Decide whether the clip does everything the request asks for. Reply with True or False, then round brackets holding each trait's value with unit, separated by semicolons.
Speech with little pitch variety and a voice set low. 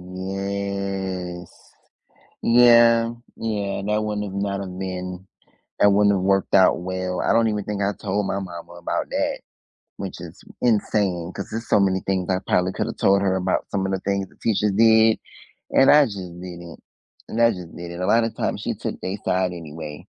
True (2.2 semitones; 95 Hz)